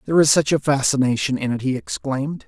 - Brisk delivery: Yes, fast, 220 wpm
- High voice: No, low, 135 Hz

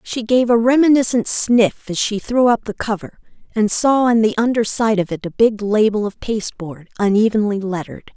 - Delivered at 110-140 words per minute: No, average, 190 wpm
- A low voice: No, high, 215 Hz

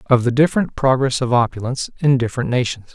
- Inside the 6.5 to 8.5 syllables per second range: Yes, 6.7 syllables/s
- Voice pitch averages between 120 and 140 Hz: Yes, low, 130 Hz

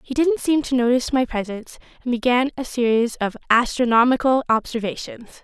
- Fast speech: No, average, 155 wpm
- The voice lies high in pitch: Yes, high, 245 Hz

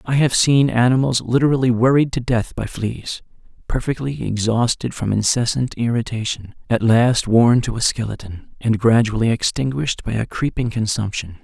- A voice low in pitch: Yes, low, 120 Hz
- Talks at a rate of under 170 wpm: Yes, average, 145 wpm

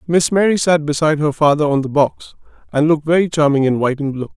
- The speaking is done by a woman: No, male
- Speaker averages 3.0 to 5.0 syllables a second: No, 6.5 syllables/s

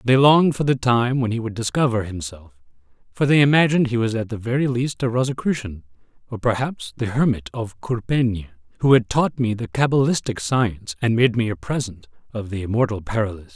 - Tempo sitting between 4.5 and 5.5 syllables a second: No, 5.8 syllables/s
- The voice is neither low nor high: No, low, 115 Hz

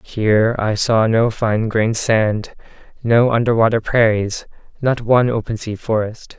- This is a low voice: Yes, low, 110 Hz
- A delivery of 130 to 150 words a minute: Yes, average, 140 wpm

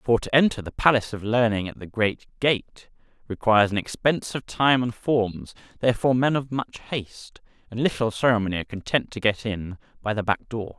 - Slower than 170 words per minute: No, average, 195 wpm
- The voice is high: No, low, 115 Hz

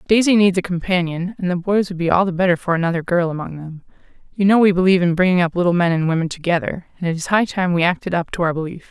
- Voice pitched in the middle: Yes, medium, 175 Hz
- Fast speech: Yes, fast, 270 wpm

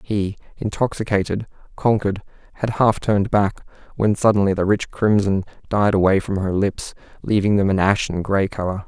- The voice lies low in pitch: Yes, low, 100 Hz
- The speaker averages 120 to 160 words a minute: Yes, average, 155 wpm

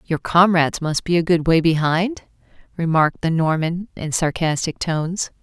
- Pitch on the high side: No, medium, 165 Hz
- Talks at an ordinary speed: Yes, average, 155 wpm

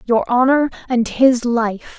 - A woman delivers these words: Yes, female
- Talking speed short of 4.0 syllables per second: Yes, 3.7 syllables/s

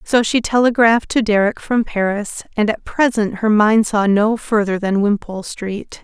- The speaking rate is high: No, average, 180 wpm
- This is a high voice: Yes, high, 215 Hz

